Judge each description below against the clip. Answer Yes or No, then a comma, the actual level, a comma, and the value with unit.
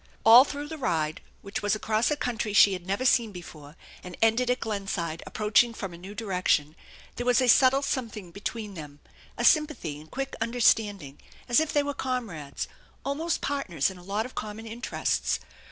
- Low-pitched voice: No, high, 215 Hz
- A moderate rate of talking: Yes, average, 185 wpm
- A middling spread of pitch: No, wide, 5.7 semitones